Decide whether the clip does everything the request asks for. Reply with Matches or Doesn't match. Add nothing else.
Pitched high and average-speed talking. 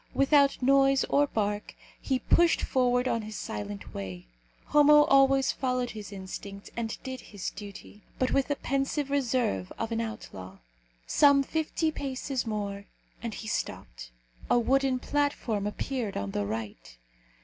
Matches